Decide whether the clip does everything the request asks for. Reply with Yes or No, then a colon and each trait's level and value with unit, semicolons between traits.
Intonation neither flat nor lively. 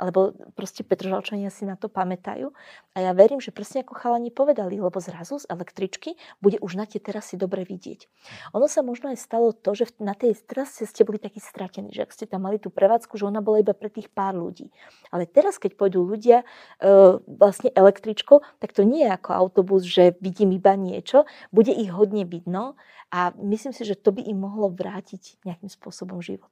Yes: average, 3.4 semitones